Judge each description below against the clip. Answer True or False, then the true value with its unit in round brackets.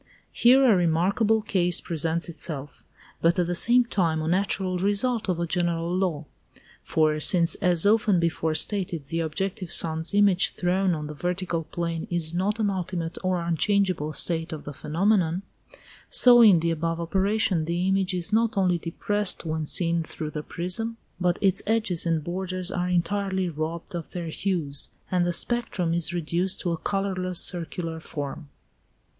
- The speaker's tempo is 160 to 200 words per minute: True (165 wpm)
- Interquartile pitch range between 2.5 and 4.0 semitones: True (2.8 semitones)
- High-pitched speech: False (175 Hz)